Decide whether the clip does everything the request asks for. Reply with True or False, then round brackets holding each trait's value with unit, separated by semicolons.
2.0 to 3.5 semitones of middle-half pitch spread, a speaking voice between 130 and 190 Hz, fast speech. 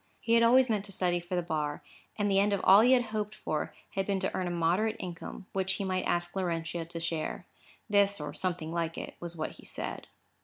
True (3.2 semitones; 185 Hz; 235 wpm)